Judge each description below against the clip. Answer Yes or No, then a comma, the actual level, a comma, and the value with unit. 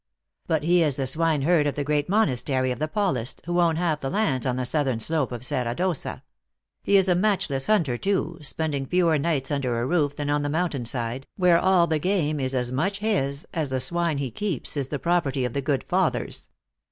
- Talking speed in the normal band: No, fast, 230 wpm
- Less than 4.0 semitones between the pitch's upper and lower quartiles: No, average, 4.5 semitones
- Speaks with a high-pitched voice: No, medium, 150 Hz